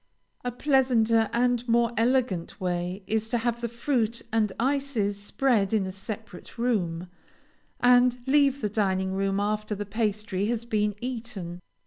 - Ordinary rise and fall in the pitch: Yes, average, 3.5 semitones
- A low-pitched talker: No, high, 220 Hz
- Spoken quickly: No, average, 145 wpm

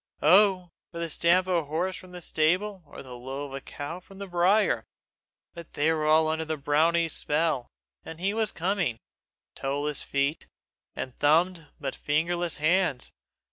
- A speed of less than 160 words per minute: No, average, 170 wpm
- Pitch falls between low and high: Yes, medium, 165 Hz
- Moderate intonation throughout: Yes, average, 3.6 semitones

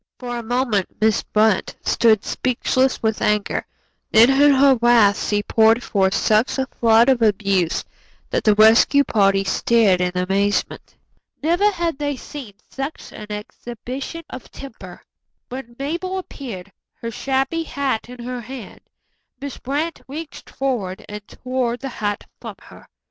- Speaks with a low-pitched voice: No, high, 235 Hz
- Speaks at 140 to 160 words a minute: Yes, average, 145 wpm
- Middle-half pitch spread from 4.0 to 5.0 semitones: Yes, average, 4.3 semitones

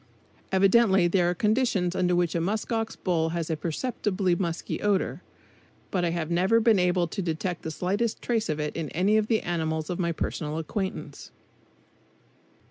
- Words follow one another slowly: No, average, 175 wpm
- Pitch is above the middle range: No, medium, 180 Hz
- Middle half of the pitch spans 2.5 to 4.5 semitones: Yes, average, 3.6 semitones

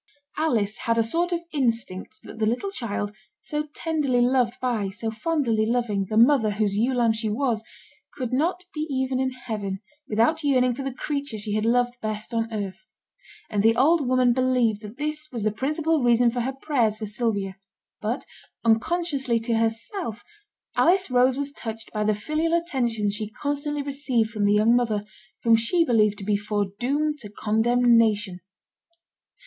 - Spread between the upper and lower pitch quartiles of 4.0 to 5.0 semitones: Yes, average, 4.3 semitones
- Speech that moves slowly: No, average, 170 wpm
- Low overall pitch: No, high, 235 Hz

